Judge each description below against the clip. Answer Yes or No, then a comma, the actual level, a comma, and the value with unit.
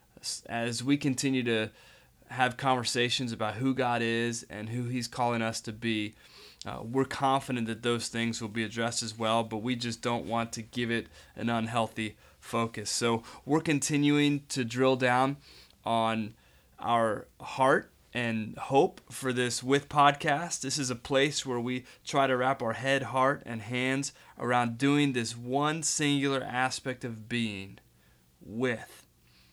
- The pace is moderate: Yes, average, 155 wpm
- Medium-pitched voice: No, low, 120 Hz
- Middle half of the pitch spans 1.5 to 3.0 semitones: Yes, average, 2.7 semitones